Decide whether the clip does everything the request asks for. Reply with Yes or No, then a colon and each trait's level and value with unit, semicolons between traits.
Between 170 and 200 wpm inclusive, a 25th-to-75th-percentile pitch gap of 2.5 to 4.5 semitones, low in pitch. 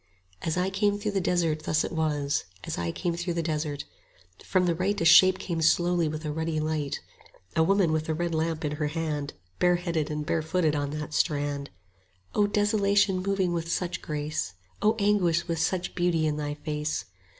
No: average, 195 wpm; average, 2.9 semitones; medium, 165 Hz